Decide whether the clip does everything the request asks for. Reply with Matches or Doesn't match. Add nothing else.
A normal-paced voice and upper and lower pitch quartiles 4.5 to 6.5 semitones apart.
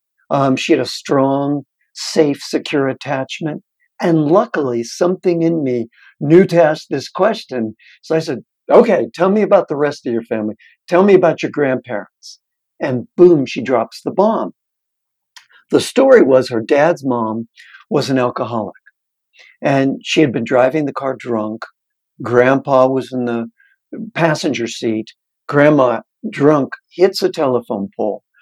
Matches